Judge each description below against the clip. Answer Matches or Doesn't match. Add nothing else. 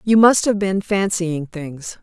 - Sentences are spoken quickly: Doesn't match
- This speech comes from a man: Doesn't match